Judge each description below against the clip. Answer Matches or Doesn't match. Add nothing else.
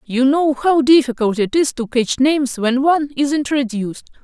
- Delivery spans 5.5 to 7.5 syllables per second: Doesn't match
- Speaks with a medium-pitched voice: Doesn't match